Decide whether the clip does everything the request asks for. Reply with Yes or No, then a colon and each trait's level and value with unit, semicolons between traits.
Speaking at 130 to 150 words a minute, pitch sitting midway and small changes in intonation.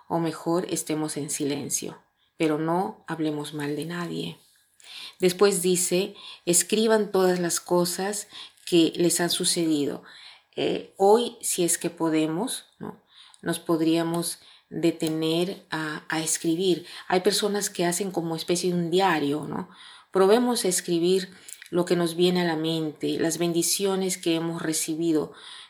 Yes: average, 140 wpm; medium, 170 Hz; narrow, 2.3 semitones